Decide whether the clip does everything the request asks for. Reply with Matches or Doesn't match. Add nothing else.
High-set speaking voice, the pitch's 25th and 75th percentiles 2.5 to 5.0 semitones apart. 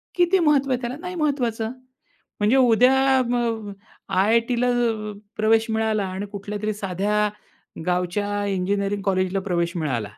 Matches